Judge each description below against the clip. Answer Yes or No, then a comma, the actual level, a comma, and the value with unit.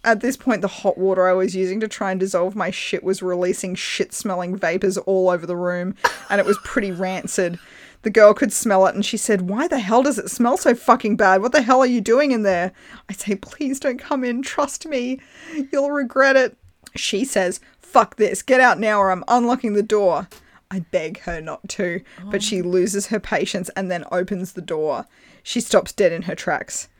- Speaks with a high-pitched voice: Yes, high, 200 Hz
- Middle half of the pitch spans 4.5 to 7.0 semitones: Yes, average, 4.8 semitones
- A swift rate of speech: Yes, fast, 220 wpm